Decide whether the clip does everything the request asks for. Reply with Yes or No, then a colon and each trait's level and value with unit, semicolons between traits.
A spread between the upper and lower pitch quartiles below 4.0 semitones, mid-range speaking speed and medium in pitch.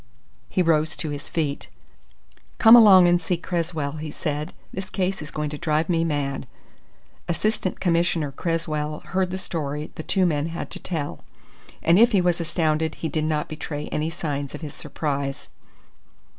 Yes: average, 2.8 semitones; average, 170 wpm; medium, 160 Hz